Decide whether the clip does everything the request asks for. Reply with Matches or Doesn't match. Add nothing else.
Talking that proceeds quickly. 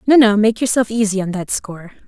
Matches